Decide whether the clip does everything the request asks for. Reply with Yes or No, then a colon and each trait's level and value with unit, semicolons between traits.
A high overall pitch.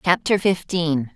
No: medium, 170 Hz